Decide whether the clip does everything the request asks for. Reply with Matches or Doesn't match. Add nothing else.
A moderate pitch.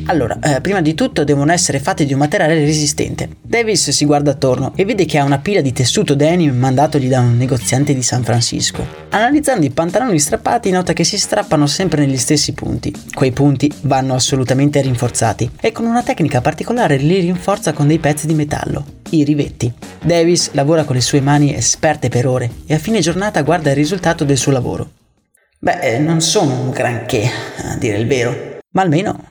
Matches